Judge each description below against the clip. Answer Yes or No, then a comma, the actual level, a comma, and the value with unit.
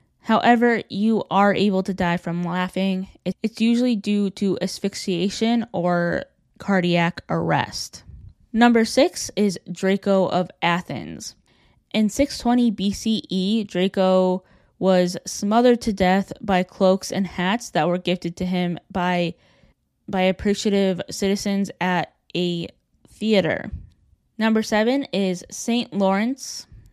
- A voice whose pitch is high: Yes, high, 195 Hz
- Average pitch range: Yes, average, 3.2 semitones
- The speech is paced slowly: Yes, slow, 115 wpm